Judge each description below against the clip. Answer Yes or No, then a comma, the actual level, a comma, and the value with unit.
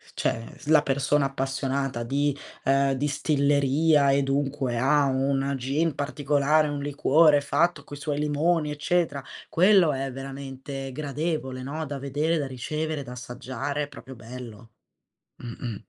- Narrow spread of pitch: Yes, narrow, 1.9 semitones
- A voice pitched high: No, medium, 140 Hz